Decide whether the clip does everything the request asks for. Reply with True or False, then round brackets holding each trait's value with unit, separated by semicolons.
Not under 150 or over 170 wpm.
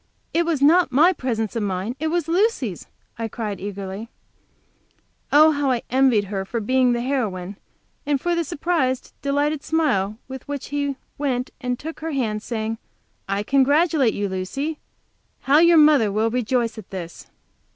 True (160 wpm)